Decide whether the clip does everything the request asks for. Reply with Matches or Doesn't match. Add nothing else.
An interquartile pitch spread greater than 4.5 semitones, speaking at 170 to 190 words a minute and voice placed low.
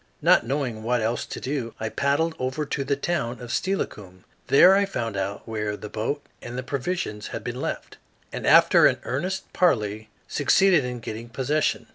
Matches